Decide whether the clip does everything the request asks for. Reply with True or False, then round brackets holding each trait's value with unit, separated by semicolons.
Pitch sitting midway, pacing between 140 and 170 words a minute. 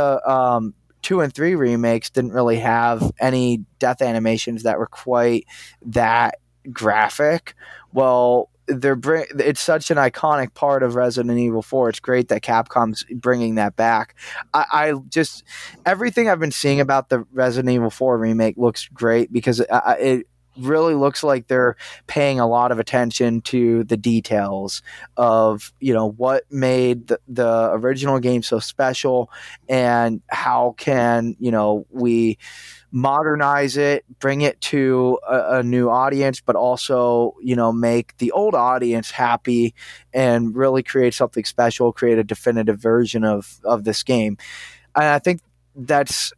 False (125 Hz; 155 wpm)